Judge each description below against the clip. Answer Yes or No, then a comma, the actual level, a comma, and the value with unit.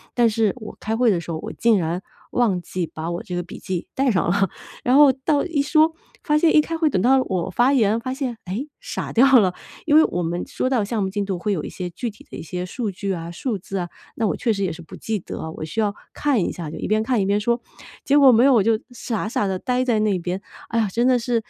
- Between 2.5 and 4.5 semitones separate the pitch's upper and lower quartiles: No, wide, 5.5 semitones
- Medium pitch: No, high, 215 Hz